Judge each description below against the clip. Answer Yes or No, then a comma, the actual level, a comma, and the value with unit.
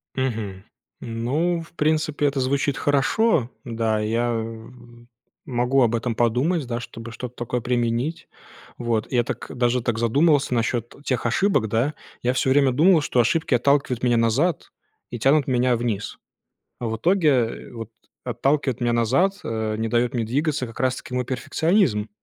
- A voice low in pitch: Yes, low, 125 Hz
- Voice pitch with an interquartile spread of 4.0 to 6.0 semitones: No, average, 3.5 semitones